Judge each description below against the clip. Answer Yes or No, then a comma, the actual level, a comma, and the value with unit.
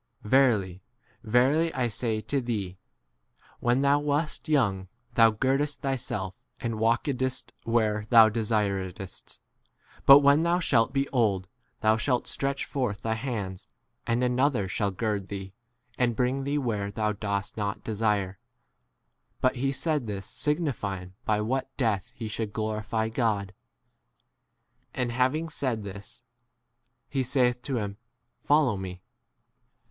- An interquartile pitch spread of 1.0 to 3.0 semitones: No, average, 4.4 semitones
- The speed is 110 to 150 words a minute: Yes, slow, 135 wpm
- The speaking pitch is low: Yes, low, 115 Hz